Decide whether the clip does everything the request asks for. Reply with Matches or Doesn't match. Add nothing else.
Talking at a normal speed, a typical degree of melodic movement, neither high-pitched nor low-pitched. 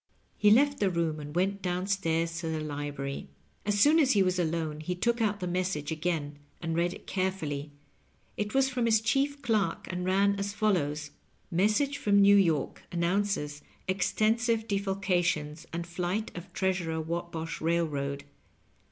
Matches